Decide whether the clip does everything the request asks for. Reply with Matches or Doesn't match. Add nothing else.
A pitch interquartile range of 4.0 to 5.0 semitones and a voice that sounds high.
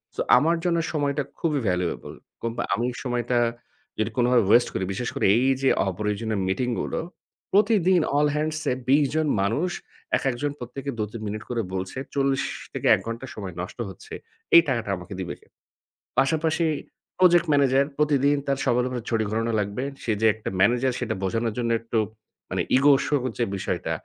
Doesn't match